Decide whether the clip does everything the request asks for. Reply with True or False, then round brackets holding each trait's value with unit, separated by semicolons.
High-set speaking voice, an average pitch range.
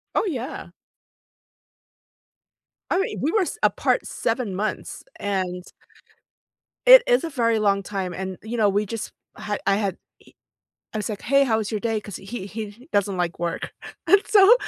True (215 Hz; 4.5 semitones)